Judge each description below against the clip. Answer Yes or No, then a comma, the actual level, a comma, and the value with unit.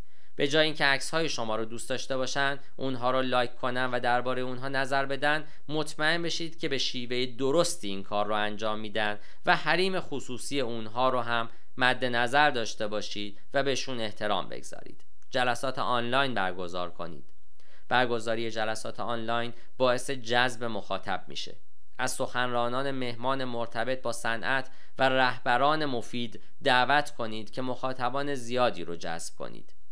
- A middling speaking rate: Yes, average, 145 wpm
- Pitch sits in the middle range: No, low, 125 Hz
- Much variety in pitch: No, average, 3.1 semitones